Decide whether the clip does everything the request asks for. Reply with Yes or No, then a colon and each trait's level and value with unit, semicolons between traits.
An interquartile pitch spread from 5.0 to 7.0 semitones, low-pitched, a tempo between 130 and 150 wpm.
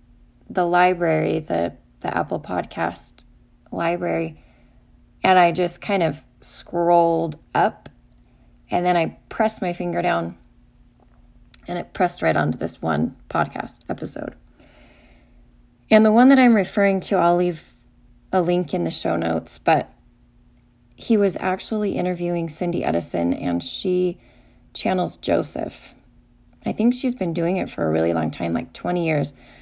No: wide, 5.4 semitones; medium, 175 Hz; average, 140 wpm